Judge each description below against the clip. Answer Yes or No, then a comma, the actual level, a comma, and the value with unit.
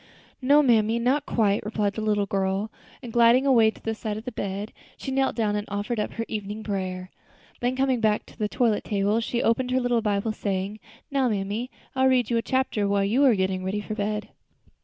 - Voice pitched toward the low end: No, high, 220 Hz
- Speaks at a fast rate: Yes, fast, 220 wpm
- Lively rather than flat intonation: No, average, 3.2 semitones